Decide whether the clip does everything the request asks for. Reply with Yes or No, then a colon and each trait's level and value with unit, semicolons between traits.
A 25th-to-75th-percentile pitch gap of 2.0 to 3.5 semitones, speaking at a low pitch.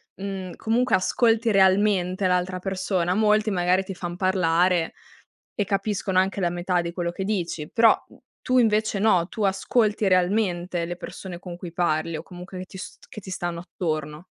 No: narrow, 2.4 semitones; medium, 185 Hz